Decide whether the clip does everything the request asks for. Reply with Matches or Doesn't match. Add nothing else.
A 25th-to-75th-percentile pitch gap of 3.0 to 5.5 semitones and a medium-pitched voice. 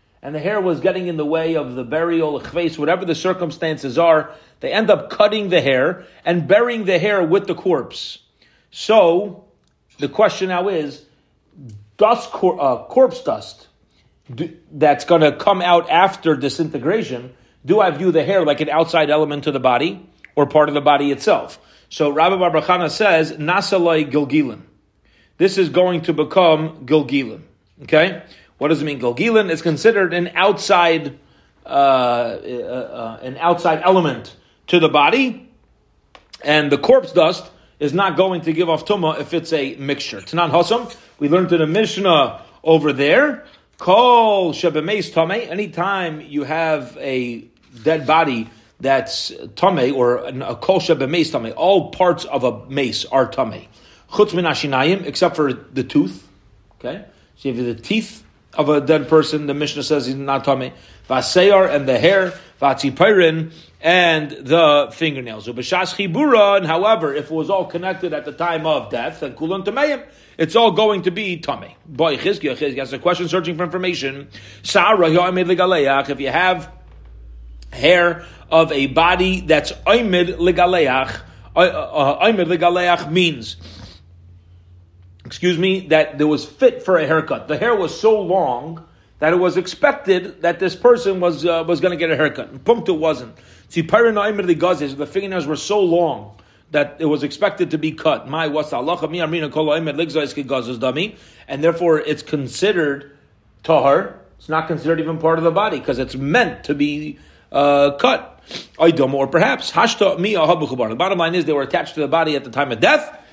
Matches